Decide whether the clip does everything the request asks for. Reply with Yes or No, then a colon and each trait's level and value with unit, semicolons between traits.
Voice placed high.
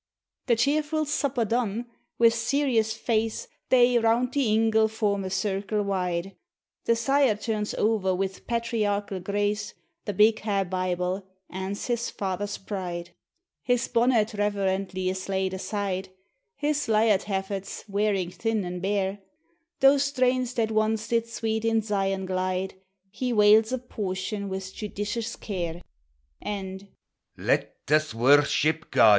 Yes: high, 210 Hz